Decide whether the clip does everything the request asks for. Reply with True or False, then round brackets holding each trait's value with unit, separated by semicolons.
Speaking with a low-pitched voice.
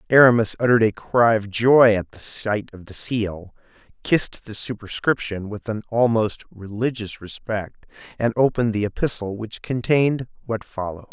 True (110 Hz)